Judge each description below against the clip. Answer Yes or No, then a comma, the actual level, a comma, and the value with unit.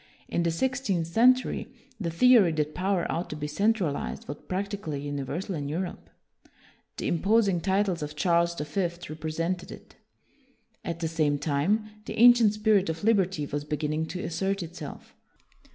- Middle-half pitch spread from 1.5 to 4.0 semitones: No, average, 4.4 semitones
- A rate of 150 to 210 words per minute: Yes, average, 160 wpm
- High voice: No, medium, 170 Hz